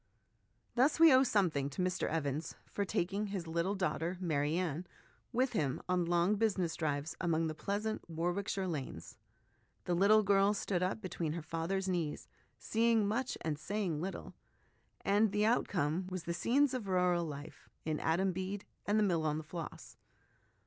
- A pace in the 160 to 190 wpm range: Yes, average, 170 wpm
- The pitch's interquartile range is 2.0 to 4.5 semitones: Yes, average, 4.0 semitones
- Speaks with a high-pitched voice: No, medium, 180 Hz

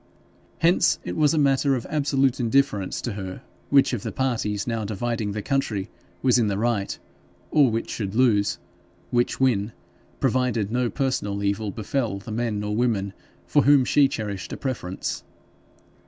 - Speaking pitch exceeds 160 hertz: No, low, 120 Hz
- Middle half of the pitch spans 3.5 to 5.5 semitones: Yes, average, 4.4 semitones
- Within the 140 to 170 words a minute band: Yes, average, 160 wpm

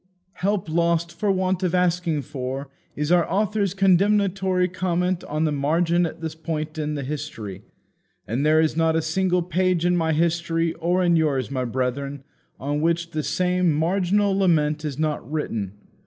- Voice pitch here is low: No, medium, 165 Hz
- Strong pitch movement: No, average, 3.2 semitones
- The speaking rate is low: No, average, 170 wpm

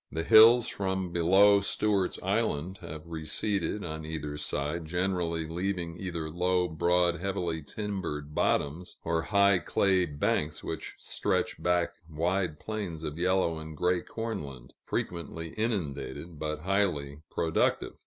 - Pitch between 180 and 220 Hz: No, very low, 85 Hz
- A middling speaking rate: No, slow, 130 wpm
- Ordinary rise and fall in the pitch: Yes, average, 3.4 semitones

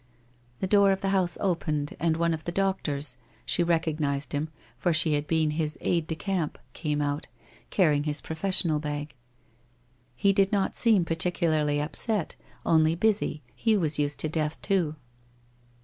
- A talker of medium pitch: Yes, medium, 160 Hz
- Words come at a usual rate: Yes, average, 170 wpm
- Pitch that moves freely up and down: No, average, 3.9 semitones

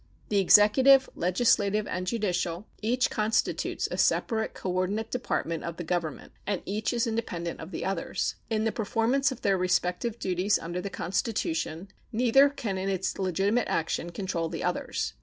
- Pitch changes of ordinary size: Yes, average, 3.9 semitones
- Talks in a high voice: Yes, high, 200 Hz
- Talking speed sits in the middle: Yes, average, 160 wpm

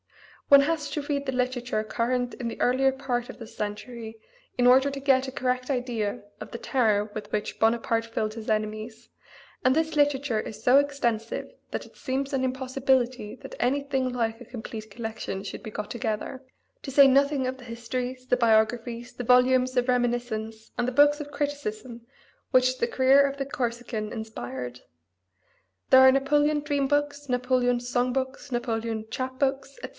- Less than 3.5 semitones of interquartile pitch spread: Yes, average, 2.9 semitones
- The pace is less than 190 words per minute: Yes, average, 175 wpm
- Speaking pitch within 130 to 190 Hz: No, very high, 250 Hz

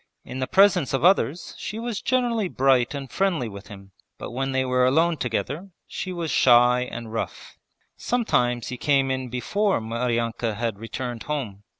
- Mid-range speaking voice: No, low, 130 Hz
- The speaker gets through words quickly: No, average, 170 wpm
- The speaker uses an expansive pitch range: Yes, wide, 6.5 semitones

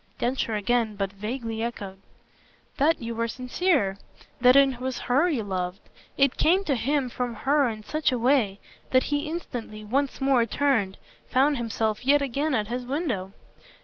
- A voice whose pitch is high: Yes, high, 245 Hz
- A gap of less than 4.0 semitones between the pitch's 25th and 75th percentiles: No, average, 4.3 semitones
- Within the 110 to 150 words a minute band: No, average, 165 wpm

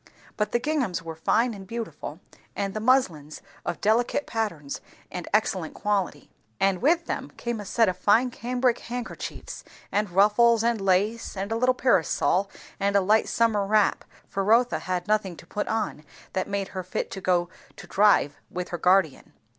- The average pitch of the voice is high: Yes, high, 205 Hz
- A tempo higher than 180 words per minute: No, average, 175 wpm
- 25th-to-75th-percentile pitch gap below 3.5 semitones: No, average, 3.9 semitones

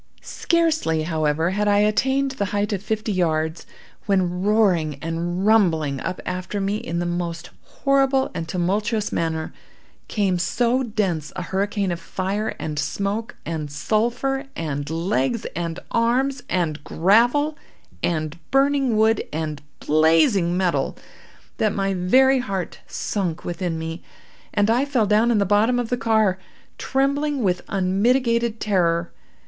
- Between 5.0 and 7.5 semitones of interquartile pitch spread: Yes, average, 5.3 semitones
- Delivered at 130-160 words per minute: Yes, average, 140 wpm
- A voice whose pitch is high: Yes, high, 195 Hz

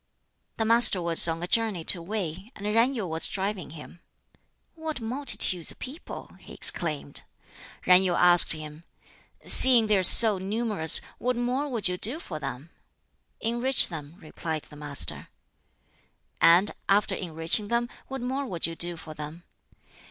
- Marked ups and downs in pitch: Yes, wide, 6.0 semitones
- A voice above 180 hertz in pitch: Yes, high, 190 Hz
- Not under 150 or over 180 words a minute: Yes, average, 160 wpm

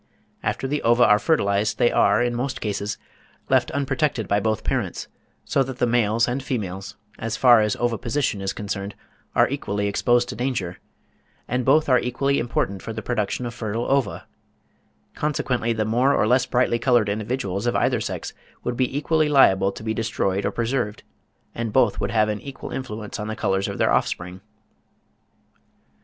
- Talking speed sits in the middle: Yes, average, 175 wpm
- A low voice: Yes, low, 115 Hz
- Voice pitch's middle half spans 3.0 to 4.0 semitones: Yes, average, 3.5 semitones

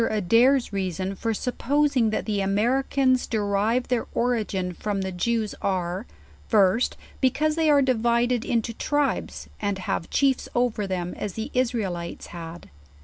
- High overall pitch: Yes, high, 225 Hz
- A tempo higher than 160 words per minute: No, average, 145 wpm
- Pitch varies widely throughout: No, average, 4.5 semitones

